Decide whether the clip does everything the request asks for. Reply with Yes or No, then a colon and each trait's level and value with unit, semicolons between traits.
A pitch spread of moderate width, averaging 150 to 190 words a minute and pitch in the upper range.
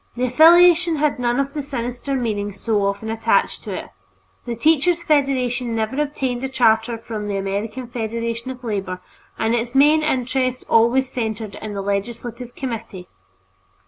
Yes: average, 3.4 semitones; average, 155 wpm; high, 240 Hz